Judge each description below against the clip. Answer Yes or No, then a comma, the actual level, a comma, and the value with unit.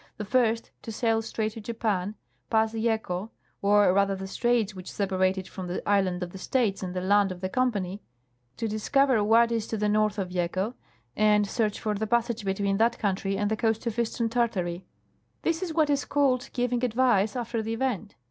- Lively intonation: No, average, 3.0 semitones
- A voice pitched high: Yes, high, 215 Hz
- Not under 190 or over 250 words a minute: Yes, average, 200 wpm